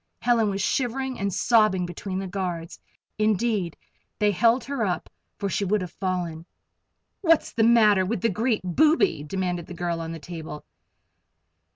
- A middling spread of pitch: Yes, average, 4.5 semitones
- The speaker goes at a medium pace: Yes, average, 160 wpm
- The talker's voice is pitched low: No, high, 195 Hz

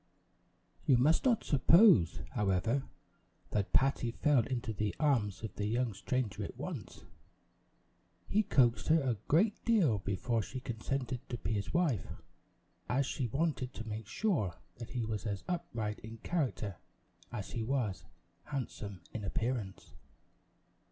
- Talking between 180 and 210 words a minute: No, average, 140 wpm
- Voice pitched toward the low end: Yes, low, 120 Hz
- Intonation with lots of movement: No, average, 4.7 semitones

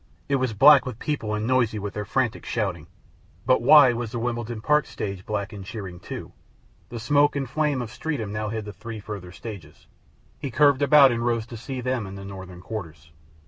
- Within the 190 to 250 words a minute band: Yes, fast, 205 wpm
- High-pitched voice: No, low, 115 Hz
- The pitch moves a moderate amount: Yes, average, 4.0 semitones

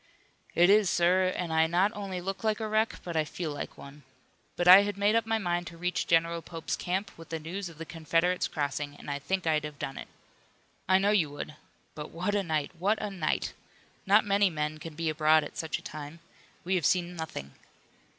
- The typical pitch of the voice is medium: Yes, medium, 175 Hz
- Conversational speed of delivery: No, fast, 220 wpm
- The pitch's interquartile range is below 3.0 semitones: No, average, 3.7 semitones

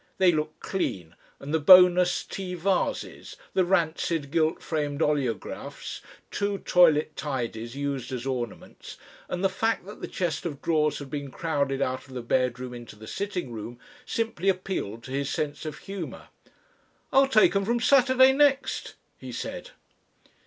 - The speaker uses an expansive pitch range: Yes, wide, 6.1 semitones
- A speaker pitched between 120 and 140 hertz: No, medium, 155 Hz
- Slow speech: No, average, 155 wpm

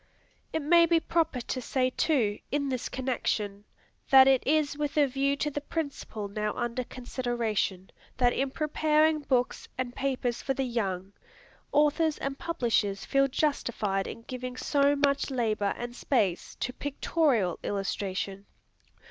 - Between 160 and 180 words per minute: No, average, 145 wpm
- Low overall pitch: No, very high, 255 Hz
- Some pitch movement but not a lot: Yes, average, 4.4 semitones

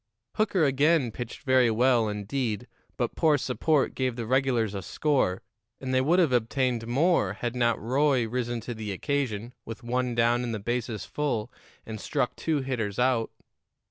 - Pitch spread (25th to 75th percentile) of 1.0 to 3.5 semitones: Yes, average, 2.9 semitones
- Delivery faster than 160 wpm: Yes, average, 170 wpm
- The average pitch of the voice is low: Yes, low, 125 Hz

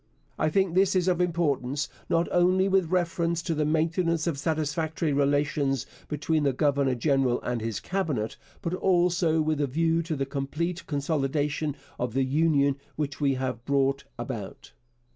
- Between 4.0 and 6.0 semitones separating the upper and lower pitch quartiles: No, average, 3.4 semitones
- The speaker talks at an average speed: Yes, average, 160 wpm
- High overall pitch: No, medium, 150 Hz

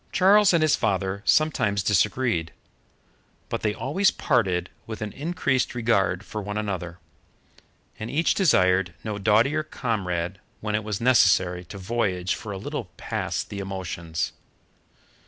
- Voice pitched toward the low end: Yes, low, 105 Hz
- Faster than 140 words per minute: No, slow, 135 wpm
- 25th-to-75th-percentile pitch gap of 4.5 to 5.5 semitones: Yes, average, 5.2 semitones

